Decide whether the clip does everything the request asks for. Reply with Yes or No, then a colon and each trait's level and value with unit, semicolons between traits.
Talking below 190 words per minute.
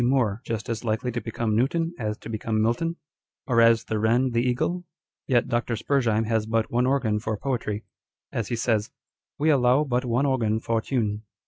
No: average, 200 wpm